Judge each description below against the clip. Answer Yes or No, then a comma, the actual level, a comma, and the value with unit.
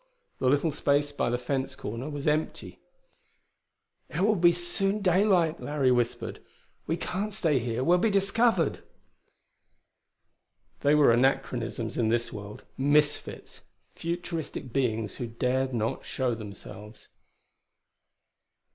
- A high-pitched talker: No, medium, 140 Hz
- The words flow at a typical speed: No, slow, 120 wpm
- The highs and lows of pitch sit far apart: Yes, wide, 6.1 semitones